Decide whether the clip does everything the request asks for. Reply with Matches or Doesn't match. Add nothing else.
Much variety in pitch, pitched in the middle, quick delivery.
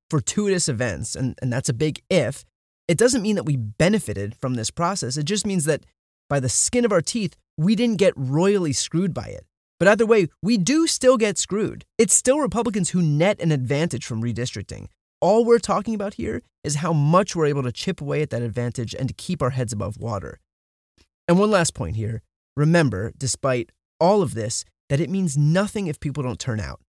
Matches